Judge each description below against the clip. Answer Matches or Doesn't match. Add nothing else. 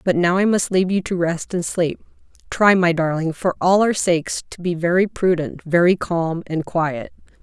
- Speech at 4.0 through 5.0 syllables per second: Matches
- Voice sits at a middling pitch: Matches